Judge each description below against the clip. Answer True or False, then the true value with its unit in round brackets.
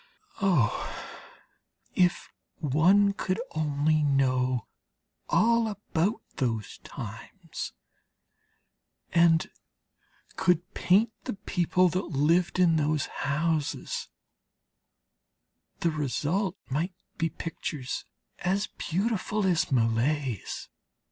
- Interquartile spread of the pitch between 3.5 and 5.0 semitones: True (4.5 semitones)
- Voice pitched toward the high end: False (165 Hz)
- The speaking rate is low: True (80 wpm)